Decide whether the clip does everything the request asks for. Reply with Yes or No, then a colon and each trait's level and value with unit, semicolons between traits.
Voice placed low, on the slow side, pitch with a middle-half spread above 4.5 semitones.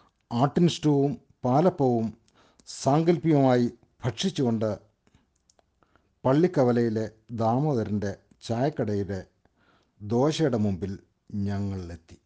Yes: low, 115 Hz; slow, 50 wpm; average, 5.0 semitones